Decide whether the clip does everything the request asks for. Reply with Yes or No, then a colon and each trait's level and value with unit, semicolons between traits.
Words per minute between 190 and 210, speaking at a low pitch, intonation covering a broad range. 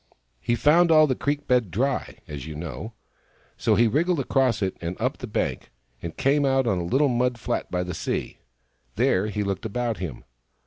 Yes: average, 195 wpm; low, 120 Hz; wide, 6.9 semitones